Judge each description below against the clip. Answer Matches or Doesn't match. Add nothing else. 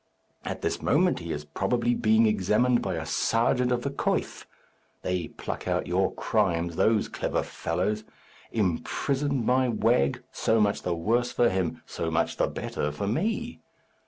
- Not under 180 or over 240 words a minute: Doesn't match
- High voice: Doesn't match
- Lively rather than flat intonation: Matches